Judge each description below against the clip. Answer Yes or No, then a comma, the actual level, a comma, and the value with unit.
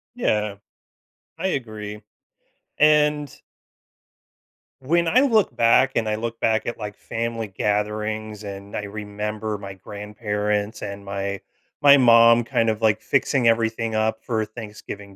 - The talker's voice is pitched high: No, low, 110 Hz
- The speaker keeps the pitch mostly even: Yes, narrow, 2.1 semitones